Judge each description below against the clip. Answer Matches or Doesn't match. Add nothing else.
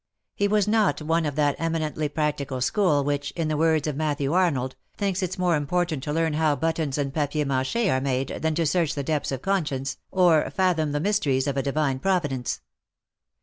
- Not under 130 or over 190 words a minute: Doesn't match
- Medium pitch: Matches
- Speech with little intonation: Doesn't match